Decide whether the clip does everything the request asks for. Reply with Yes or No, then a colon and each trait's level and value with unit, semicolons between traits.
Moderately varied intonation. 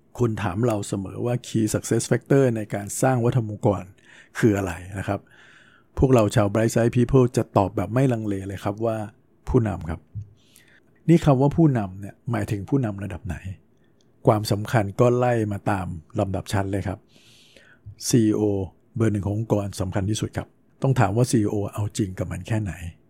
Yes: average, 3.4 semitones